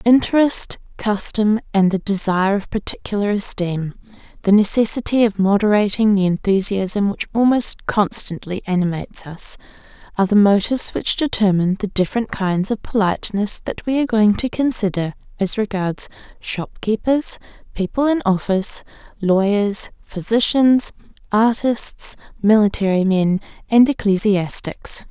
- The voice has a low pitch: No, high, 210 Hz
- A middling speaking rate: No, slow, 110 wpm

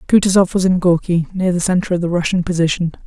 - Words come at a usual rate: No, fast, 215 wpm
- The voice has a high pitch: No, medium, 180 Hz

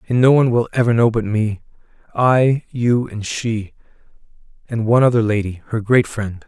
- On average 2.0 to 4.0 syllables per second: No, 5.0 syllables/s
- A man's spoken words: Yes, male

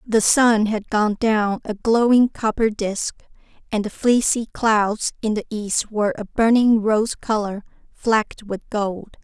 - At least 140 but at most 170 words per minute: Yes, average, 155 wpm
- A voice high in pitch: Yes, high, 215 Hz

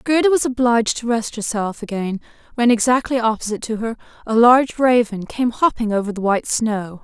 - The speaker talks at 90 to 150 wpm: No, average, 180 wpm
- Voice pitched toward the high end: Yes, high, 230 Hz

